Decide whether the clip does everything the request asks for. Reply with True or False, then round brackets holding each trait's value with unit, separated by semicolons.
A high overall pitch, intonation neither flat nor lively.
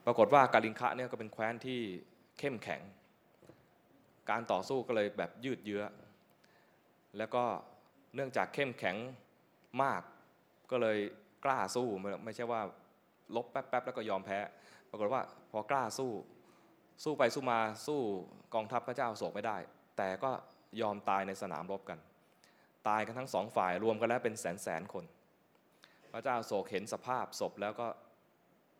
False (110 Hz; 3.7 semitones)